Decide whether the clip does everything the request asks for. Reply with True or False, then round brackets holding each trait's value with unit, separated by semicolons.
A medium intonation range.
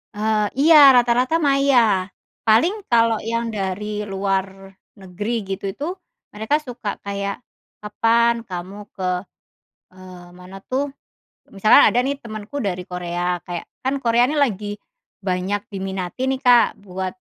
True (4.0 semitones)